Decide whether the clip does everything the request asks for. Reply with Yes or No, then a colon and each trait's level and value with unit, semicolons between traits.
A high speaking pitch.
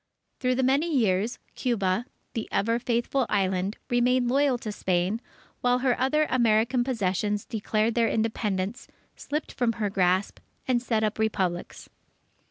Yes: high, 230 Hz